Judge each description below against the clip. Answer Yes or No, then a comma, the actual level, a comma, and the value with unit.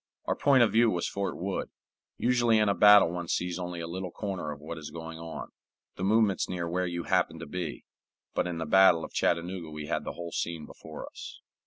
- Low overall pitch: Yes, very low, 90 Hz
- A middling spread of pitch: Yes, average, 3.0 semitones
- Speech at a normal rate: No, fast, 220 wpm